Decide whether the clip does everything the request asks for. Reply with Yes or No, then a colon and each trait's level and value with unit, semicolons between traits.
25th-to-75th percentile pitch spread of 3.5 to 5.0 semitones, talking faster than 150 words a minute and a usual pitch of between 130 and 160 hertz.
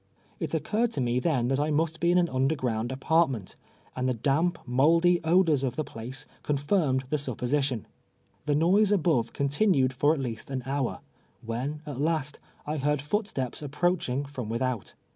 Yes: average, 4.0 semitones; average, 170 wpm; medium, 140 Hz